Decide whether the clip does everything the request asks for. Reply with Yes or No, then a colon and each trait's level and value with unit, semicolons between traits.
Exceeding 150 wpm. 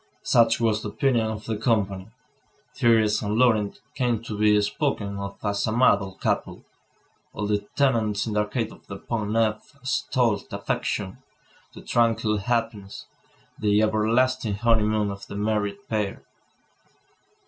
No: average, 145 wpm